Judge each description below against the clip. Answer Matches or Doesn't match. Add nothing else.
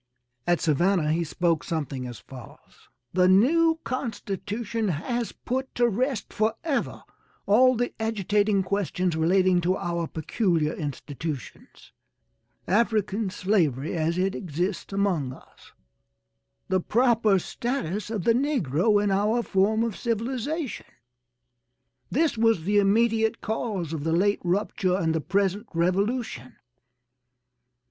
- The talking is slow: Matches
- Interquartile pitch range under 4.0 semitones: Doesn't match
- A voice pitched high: Matches